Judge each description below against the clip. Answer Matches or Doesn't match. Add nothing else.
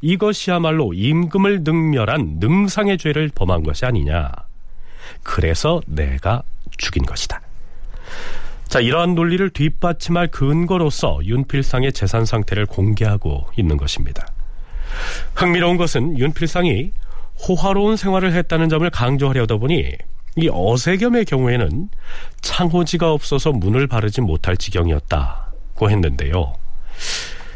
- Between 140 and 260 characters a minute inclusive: Doesn't match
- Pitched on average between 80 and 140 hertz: Matches